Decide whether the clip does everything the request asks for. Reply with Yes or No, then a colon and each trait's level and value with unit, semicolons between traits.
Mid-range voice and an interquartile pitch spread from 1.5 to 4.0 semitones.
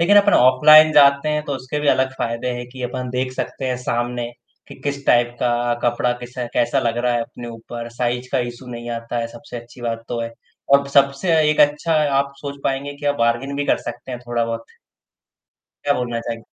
No: low, 125 Hz; average, 2.9 semitones